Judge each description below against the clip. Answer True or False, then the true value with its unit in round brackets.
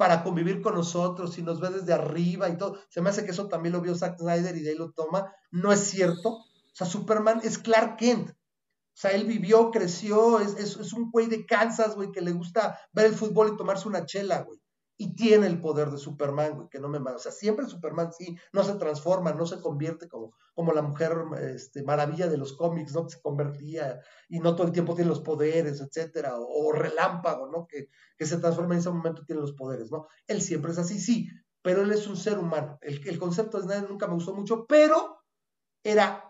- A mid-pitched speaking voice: True (180 Hz)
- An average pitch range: True (4.1 semitones)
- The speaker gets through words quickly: True (235 wpm)